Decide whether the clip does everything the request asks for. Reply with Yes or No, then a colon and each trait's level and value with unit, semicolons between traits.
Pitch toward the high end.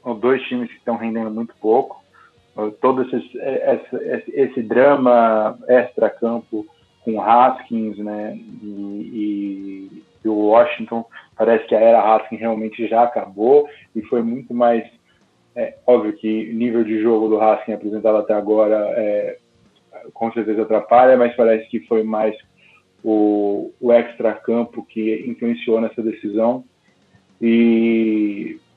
No: low, 115 Hz